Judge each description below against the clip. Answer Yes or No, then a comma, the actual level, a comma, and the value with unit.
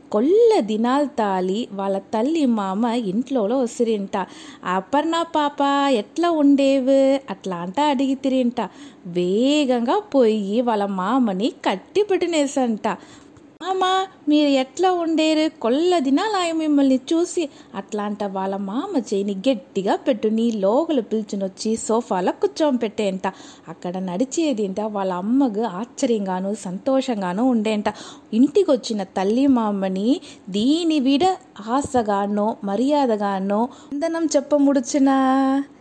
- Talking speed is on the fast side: No, average, 90 wpm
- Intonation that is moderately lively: No, wide, 5.8 semitones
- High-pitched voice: Yes, very high, 260 Hz